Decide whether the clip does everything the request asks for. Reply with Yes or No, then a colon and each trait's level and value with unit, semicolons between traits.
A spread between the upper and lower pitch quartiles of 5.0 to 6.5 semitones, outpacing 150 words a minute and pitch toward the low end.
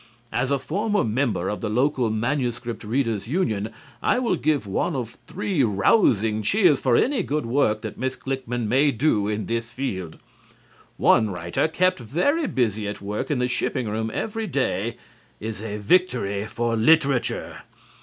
Yes: average, 5.3 semitones; average, 160 wpm; low, 120 Hz